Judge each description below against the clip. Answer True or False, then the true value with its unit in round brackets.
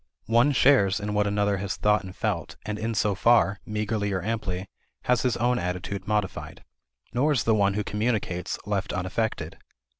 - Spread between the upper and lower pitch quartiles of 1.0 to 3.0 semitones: True (2.5 semitones)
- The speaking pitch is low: True (105 Hz)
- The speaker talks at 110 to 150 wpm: False (175 wpm)